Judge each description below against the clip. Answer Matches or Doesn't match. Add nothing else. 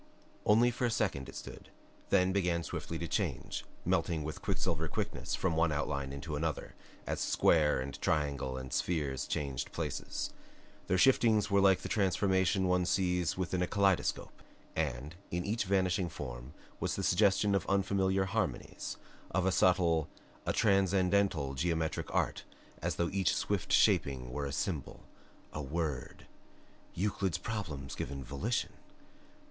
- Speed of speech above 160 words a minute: Doesn't match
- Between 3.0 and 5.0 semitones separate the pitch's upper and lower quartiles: Matches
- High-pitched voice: Doesn't match